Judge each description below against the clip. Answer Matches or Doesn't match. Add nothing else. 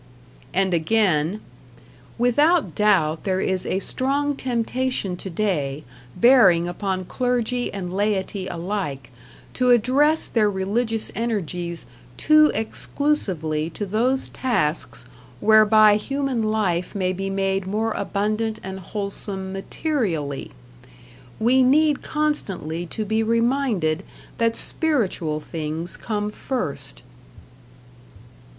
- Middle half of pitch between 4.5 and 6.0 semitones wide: Matches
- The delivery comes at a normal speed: Doesn't match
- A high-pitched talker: Matches